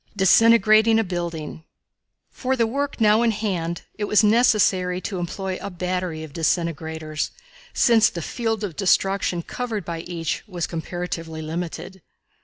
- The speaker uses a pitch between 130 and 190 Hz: Yes, medium, 185 Hz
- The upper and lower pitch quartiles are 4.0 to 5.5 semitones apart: Yes, average, 4.5 semitones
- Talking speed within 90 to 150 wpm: Yes, average, 140 wpm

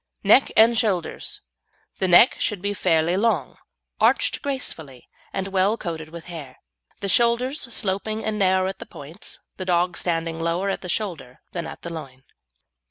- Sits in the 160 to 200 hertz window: Yes, medium, 185 Hz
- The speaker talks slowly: No, average, 165 wpm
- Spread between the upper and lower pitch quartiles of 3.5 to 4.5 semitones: Yes, average, 4.2 semitones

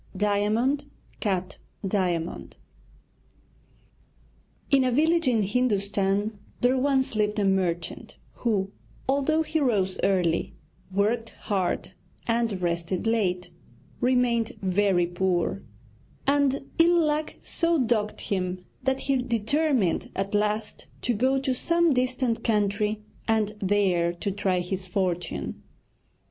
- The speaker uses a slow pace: Yes, slow, 110 wpm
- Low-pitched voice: No, high, 210 Hz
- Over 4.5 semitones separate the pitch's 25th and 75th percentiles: Yes, average, 5.2 semitones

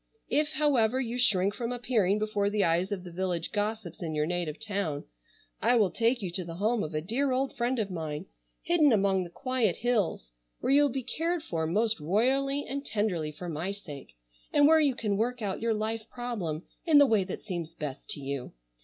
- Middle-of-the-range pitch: No, high, 210 Hz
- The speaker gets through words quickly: Yes, fast, 210 wpm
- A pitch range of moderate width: No, wide, 6.0 semitones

